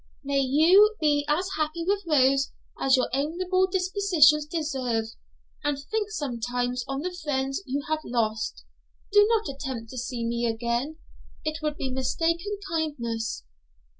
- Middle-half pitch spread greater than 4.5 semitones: Yes, average, 5.0 semitones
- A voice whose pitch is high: Yes, very high, 290 Hz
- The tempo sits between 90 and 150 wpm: Yes, average, 140 wpm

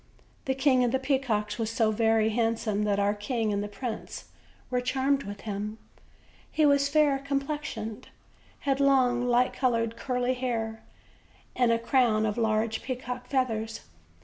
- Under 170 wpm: Yes, average, 155 wpm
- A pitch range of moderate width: Yes, average, 3.2 semitones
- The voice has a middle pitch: No, high, 240 Hz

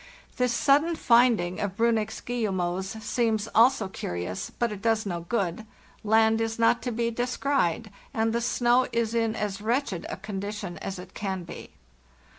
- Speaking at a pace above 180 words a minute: No, average, 170 wpm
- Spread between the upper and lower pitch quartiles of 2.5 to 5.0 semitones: Yes, average, 3.3 semitones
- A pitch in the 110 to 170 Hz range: No, high, 220 Hz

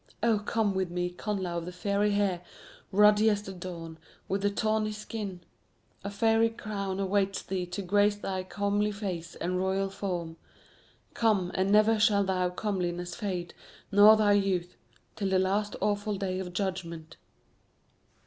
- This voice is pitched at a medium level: No, high, 195 Hz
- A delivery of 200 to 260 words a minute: No, average, 155 wpm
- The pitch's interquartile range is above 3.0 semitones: No, narrow, 2.4 semitones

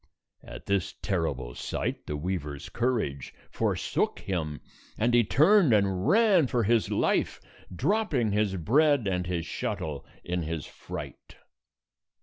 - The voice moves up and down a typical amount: No, wide, 6.9 semitones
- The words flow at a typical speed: No, slow, 130 wpm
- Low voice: Yes, low, 100 Hz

